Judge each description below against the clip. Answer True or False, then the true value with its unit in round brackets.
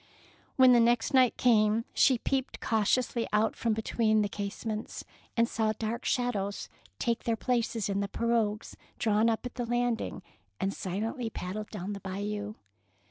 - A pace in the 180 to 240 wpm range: False (160 wpm)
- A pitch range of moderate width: False (2.3 semitones)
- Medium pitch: False (225 Hz)